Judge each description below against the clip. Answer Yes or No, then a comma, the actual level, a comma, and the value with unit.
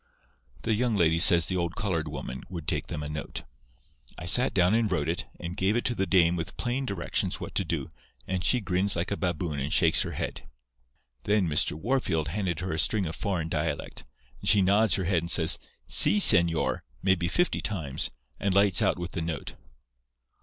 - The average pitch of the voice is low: Yes, very low, 90 Hz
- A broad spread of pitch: No, average, 3.5 semitones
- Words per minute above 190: Yes, fast, 205 wpm